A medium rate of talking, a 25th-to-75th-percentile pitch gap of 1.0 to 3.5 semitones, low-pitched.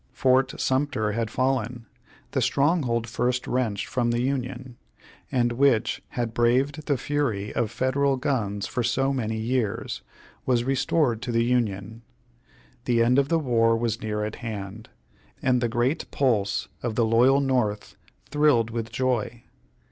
Yes: average, 150 wpm; narrow, 2.6 semitones; low, 120 Hz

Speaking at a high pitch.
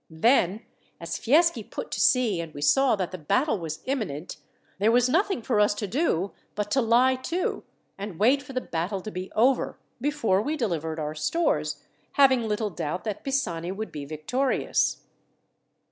Yes: high, 215 Hz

